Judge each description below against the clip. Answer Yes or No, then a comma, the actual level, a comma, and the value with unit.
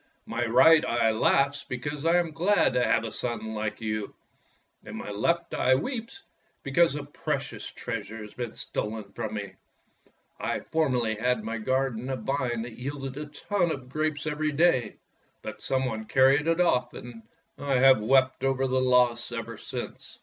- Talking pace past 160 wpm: Yes, average, 175 wpm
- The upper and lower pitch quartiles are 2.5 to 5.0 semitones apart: Yes, average, 4.3 semitones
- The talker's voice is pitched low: Yes, low, 130 Hz